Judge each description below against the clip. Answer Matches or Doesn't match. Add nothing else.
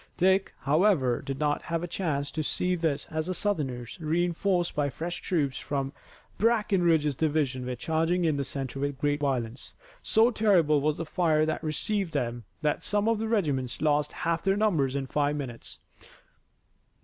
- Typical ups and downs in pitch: Matches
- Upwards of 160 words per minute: Matches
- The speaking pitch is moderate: Matches